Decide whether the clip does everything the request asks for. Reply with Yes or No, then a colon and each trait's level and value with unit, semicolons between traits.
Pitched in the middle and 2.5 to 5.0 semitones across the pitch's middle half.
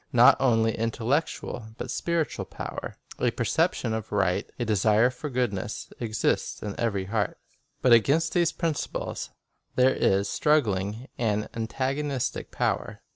No: low, 115 Hz; average, 4.1 semitones